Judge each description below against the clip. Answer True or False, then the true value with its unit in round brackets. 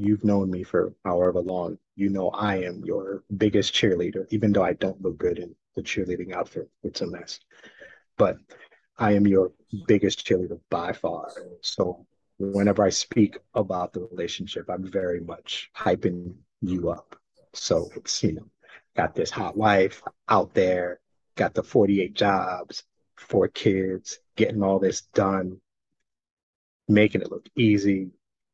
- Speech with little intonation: True (2.0 semitones)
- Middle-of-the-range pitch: False (95 Hz)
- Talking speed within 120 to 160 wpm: True (150 wpm)